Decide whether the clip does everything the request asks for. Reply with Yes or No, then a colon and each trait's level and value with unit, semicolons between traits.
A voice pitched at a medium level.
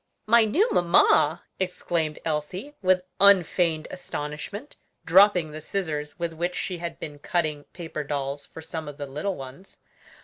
Yes: medium, 165 Hz